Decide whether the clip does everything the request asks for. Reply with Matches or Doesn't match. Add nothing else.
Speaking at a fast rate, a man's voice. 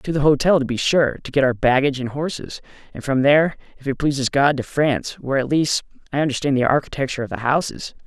Matches